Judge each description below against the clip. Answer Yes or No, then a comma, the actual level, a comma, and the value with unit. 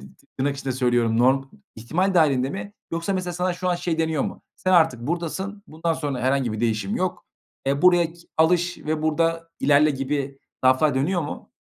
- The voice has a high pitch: No, medium, 155 Hz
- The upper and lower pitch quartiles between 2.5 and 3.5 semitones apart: No, average, 4.6 semitones